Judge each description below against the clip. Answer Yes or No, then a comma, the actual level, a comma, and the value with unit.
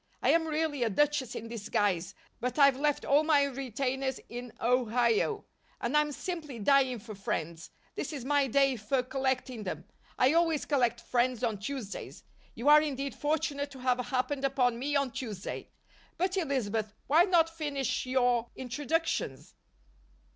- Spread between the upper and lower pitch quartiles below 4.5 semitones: Yes, average, 3.5 semitones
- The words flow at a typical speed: Yes, average, 155 wpm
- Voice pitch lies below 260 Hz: No, very high, 265 Hz